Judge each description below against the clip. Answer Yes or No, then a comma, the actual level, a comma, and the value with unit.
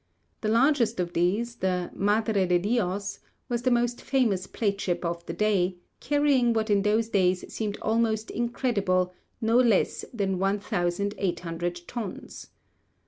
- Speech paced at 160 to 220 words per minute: No, average, 140 wpm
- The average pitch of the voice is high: Yes, high, 205 Hz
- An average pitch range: Yes, average, 4.2 semitones